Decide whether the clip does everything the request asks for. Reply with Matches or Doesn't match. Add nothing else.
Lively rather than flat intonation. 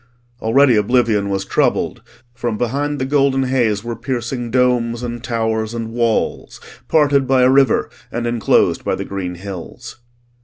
Doesn't match